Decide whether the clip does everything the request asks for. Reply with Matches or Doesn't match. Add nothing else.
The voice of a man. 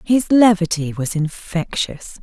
Doesn't match